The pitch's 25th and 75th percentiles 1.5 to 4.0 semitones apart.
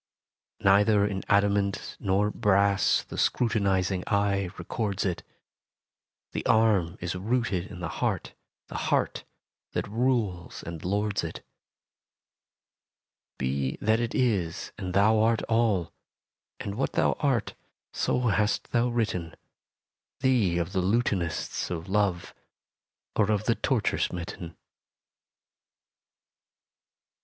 Yes: average, 3.4 semitones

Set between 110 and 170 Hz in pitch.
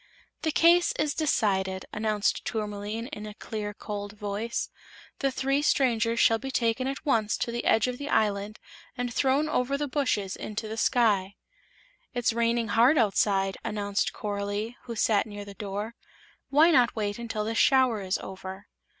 No: high, 220 Hz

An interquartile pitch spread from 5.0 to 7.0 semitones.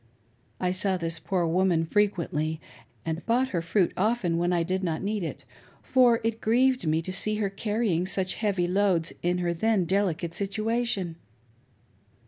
No: average, 4.0 semitones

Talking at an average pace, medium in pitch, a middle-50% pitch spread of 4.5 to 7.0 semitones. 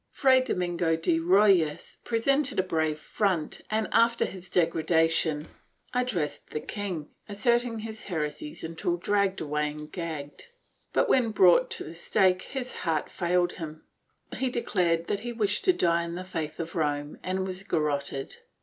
Yes: average, 160 wpm; medium, 175 Hz; average, 4.8 semitones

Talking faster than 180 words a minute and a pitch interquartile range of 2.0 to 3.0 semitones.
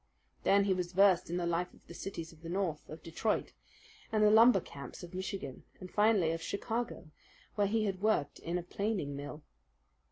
No: average, 195 wpm; average, 3.6 semitones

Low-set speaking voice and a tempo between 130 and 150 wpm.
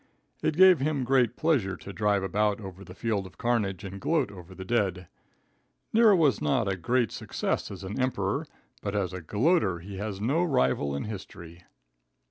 No: low, 105 Hz; average, 180 wpm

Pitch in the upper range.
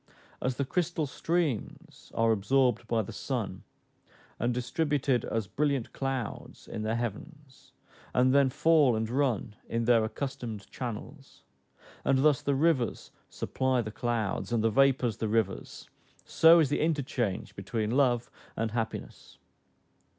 No: low, 125 Hz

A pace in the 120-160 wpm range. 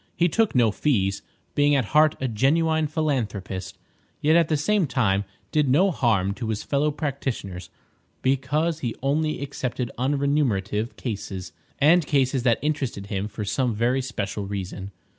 Yes: average, 150 wpm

